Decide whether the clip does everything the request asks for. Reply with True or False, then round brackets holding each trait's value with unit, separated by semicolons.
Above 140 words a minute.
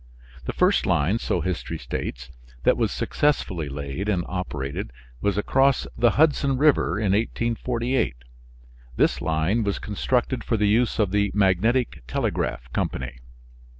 False (135 wpm)